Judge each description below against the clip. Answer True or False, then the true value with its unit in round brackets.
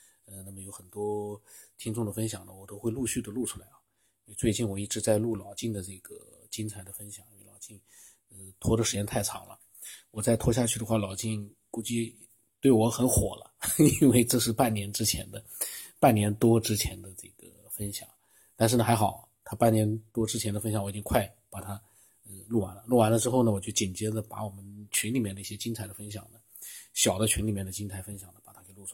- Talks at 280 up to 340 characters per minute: True (310 characters per minute)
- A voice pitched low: True (110 Hz)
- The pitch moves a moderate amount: False (2.2 semitones)